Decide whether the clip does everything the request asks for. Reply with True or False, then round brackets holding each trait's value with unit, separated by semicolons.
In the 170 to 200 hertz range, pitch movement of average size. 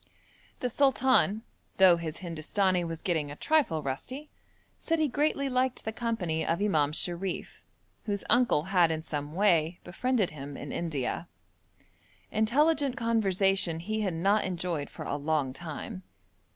False (185 Hz; 6.3 semitones)